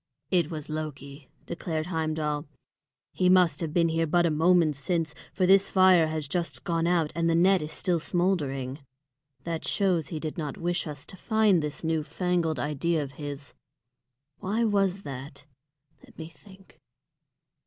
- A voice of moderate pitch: Yes, medium, 165 Hz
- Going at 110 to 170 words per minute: Yes, average, 165 wpm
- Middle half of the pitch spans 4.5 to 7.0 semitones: No, average, 3.0 semitones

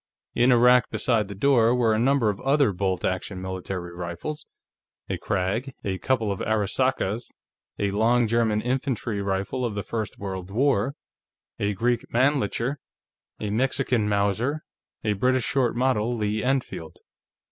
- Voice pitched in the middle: No, low, 110 Hz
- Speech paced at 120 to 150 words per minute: Yes, average, 145 wpm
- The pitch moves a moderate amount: Yes, average, 4.1 semitones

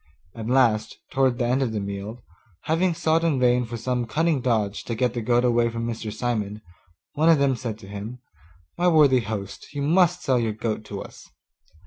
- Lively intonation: No, average, 3.7 semitones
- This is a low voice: Yes, low, 120 Hz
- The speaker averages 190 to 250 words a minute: Yes, average, 200 wpm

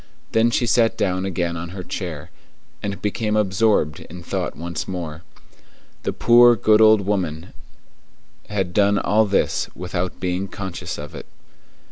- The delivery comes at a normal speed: Yes, average, 145 wpm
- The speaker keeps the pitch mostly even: No, average, 3.5 semitones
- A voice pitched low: Yes, very low, 95 Hz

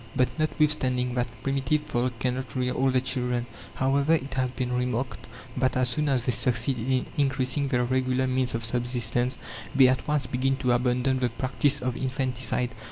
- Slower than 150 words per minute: No, average, 175 wpm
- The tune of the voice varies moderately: No, narrow, 1.3 semitones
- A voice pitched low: Yes, low, 130 Hz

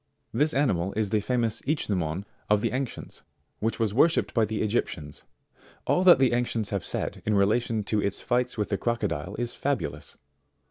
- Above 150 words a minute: Yes, average, 175 wpm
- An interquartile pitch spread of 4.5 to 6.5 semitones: No, average, 3.5 semitones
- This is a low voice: Yes, low, 110 Hz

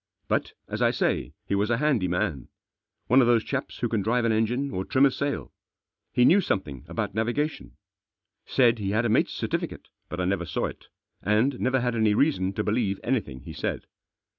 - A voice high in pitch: No, low, 115 Hz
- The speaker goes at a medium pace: No, fast, 210 wpm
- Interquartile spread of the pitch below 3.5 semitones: No, average, 4.5 semitones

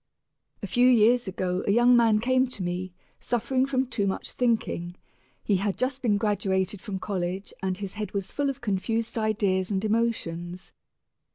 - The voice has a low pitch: No, high, 210 Hz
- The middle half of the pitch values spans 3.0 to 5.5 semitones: Yes, average, 4.1 semitones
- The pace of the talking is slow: No, average, 170 wpm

